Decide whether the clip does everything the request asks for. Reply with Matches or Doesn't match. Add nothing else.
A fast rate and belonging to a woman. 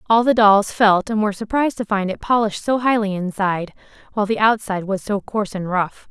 Matches